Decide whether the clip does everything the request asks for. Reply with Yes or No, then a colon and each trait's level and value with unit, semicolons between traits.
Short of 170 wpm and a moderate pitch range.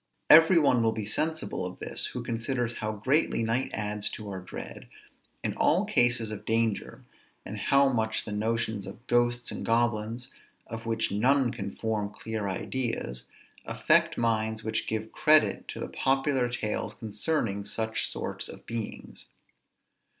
No: average, 150 wpm; narrow, 2.3 semitones